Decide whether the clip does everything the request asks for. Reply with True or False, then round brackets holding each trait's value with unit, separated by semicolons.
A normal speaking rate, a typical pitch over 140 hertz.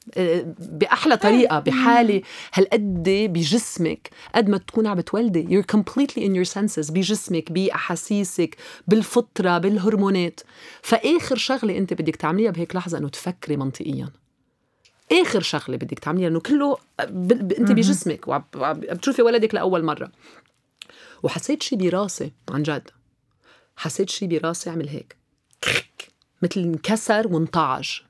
True (120 wpm; 190 Hz)